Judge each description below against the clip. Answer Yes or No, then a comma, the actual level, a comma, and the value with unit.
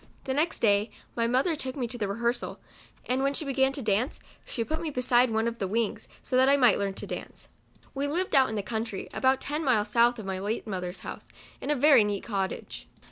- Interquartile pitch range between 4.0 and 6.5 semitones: Yes, average, 4.3 semitones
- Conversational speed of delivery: No, fast, 235 wpm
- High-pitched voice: Yes, high, 240 Hz